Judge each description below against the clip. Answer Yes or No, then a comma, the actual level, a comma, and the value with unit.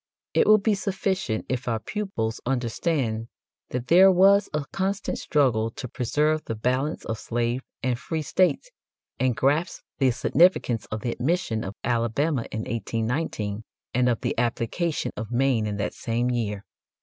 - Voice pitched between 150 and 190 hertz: No, low, 125 Hz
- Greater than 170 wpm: No, average, 155 wpm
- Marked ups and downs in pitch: Yes, wide, 6.1 semitones